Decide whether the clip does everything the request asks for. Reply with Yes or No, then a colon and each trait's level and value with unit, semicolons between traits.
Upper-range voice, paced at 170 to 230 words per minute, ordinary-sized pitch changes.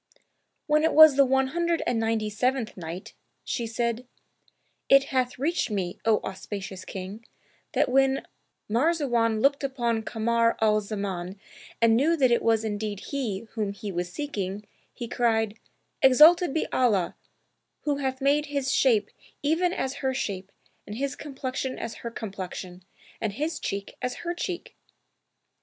No: high, 235 Hz; average, 150 wpm; average, 4.7 semitones